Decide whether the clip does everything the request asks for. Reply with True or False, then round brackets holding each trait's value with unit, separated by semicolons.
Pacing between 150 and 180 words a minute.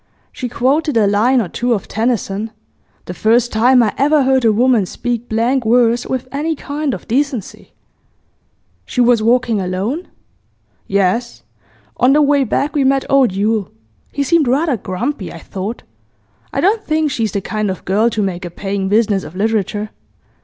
True (170 wpm)